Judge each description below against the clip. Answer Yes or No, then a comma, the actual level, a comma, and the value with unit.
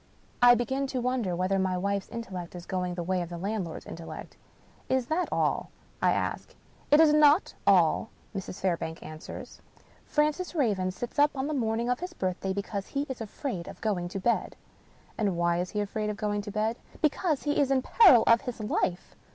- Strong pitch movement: Yes, wide, 6.3 semitones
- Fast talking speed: Yes, fast, 215 wpm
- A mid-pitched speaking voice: No, high, 215 Hz